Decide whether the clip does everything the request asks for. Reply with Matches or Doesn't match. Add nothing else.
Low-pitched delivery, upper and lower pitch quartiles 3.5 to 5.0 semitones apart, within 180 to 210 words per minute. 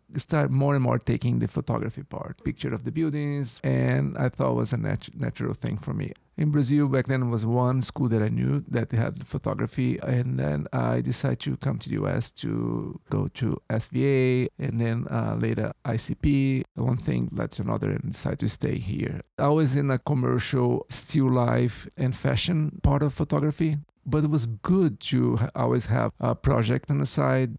Matches